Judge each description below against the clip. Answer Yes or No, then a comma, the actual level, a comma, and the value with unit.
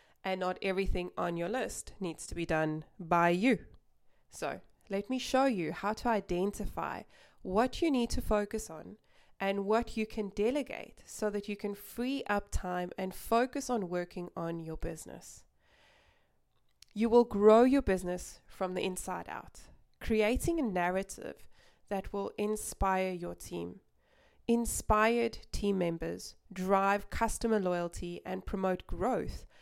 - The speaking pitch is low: No, high, 200 Hz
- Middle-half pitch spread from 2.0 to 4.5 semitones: Yes, average, 3.8 semitones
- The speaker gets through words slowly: No, average, 145 wpm